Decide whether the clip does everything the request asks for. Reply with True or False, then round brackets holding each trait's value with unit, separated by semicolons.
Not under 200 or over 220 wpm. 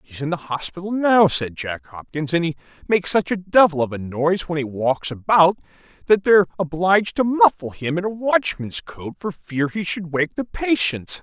True (205 wpm)